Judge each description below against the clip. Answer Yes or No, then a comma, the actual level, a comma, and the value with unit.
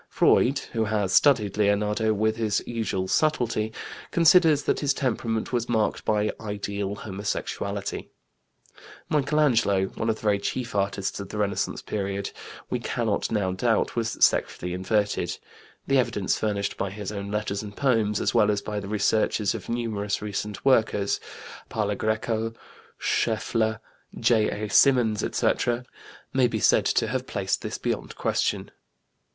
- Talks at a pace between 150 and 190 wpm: No, average, 140 wpm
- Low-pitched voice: Yes, low, 110 Hz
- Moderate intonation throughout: No, narrow, 2.3 semitones